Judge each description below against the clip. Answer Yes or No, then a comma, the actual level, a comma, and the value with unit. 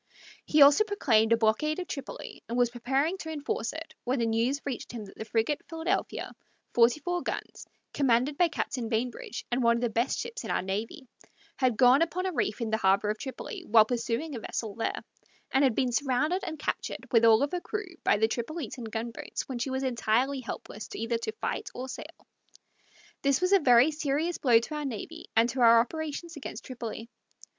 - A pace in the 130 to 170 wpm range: No, average, 200 wpm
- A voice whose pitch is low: No, very high, 250 Hz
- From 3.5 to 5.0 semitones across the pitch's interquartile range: Yes, average, 4.7 semitones